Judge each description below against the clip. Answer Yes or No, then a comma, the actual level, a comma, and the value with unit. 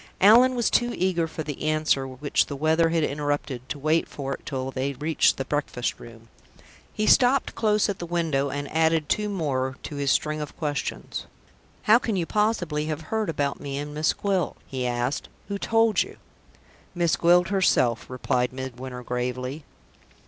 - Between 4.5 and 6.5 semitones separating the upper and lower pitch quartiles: Yes, average, 4.8 semitones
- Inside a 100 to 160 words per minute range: No, average, 175 wpm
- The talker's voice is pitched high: No, medium, 150 Hz